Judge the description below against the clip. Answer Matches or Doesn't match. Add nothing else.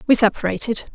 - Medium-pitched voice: Doesn't match